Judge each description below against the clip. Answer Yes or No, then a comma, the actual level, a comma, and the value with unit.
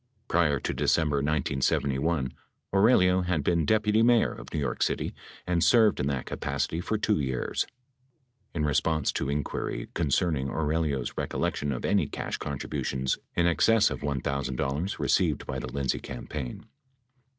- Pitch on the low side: Yes, very low, 75 Hz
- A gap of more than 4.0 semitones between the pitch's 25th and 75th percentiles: Yes, average, 4.4 semitones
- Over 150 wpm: No, average, 145 wpm